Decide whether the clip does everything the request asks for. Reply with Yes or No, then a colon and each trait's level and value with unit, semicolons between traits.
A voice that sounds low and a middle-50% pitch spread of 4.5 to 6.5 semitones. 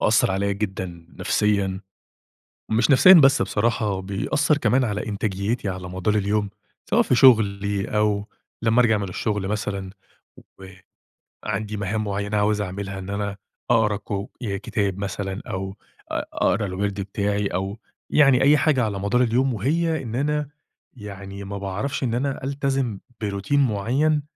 No: low, 105 Hz; average, 3.7 semitones